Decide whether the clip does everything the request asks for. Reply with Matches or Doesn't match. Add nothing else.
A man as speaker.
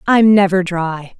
Doesn't match